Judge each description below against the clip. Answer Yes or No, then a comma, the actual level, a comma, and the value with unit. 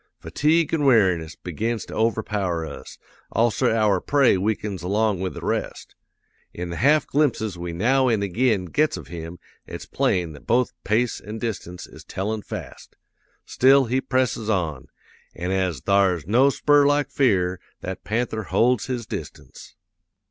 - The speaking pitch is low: Yes, low, 110 Hz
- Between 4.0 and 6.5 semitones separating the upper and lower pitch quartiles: Yes, wide, 5.5 semitones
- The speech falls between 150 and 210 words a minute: Yes, average, 155 wpm